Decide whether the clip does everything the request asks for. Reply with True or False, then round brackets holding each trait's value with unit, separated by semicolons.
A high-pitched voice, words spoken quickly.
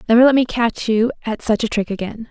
True (230 Hz; 260 wpm)